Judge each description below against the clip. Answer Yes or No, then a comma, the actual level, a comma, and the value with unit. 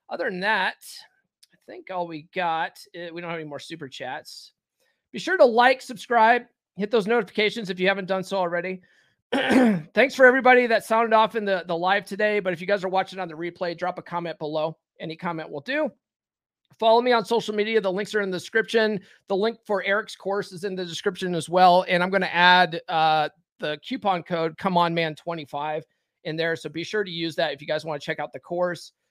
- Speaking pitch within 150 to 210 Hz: Yes, medium, 185 Hz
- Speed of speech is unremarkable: No, fast, 225 wpm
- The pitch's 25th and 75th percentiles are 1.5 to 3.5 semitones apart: No, average, 4.3 semitones